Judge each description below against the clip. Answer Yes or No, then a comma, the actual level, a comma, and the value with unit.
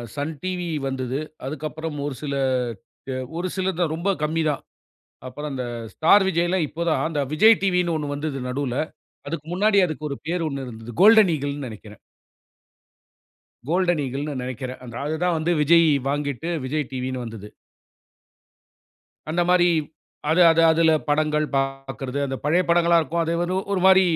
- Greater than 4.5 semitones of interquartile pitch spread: No, average, 4.1 semitones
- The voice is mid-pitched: Yes, medium, 155 Hz